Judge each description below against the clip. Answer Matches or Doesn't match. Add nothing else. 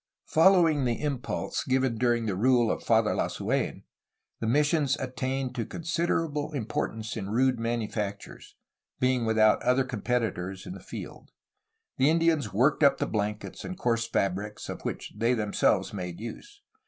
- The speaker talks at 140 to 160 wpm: Matches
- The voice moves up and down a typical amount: Matches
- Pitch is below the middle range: Matches